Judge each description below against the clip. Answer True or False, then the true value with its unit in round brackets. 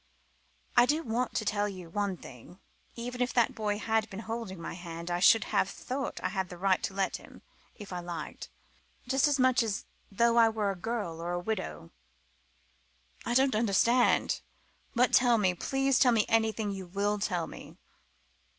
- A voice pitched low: False (210 Hz)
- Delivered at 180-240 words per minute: True (185 wpm)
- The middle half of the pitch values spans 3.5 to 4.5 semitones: True (4.2 semitones)